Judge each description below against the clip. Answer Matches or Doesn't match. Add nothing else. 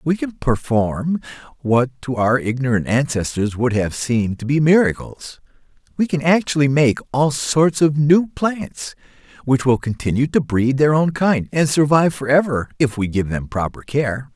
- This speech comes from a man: Matches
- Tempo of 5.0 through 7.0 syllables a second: Doesn't match